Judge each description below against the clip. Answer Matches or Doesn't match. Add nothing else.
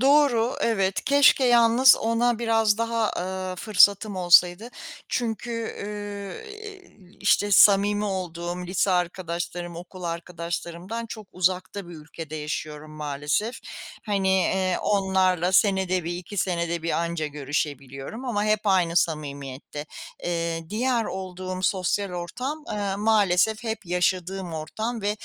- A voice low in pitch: Doesn't match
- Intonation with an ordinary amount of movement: Matches